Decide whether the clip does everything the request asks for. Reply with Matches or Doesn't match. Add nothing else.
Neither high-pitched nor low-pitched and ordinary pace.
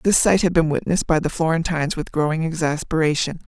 Matches